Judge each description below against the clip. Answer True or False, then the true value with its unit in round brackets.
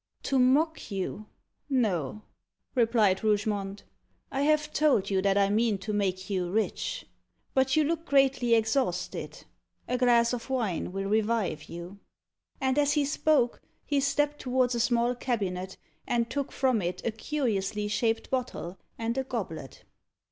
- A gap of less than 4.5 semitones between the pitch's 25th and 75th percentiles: False (5.0 semitones)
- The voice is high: True (230 Hz)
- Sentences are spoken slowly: False (150 wpm)